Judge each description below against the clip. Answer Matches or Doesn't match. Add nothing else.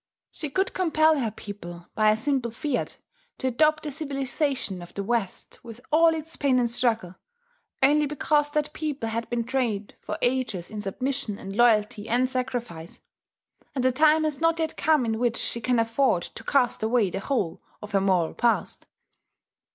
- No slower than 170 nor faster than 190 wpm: Matches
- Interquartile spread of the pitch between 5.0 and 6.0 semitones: Matches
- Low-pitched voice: Doesn't match